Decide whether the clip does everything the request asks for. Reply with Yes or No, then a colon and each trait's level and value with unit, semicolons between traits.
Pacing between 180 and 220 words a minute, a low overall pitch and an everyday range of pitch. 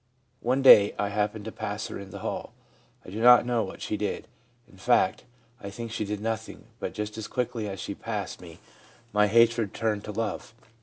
No: fast, 205 wpm; low, 105 Hz; narrow, 2.1 semitones